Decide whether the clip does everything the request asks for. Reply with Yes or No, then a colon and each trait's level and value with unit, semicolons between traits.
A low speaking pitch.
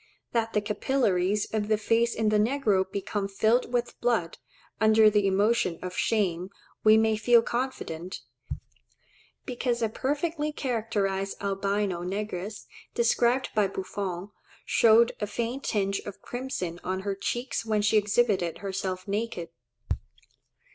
No: high, 210 Hz